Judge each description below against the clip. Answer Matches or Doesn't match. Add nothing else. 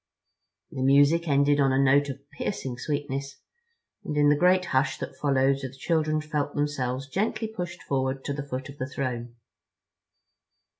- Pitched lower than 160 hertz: Matches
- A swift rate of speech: Doesn't match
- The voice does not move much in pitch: Matches